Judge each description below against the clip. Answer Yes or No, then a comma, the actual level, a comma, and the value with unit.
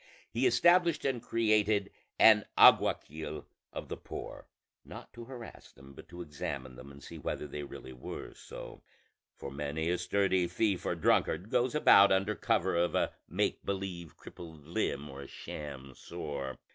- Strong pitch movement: Yes, wide, 6.8 semitones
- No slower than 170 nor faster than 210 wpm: No, average, 160 wpm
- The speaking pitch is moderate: No, very low, 85 Hz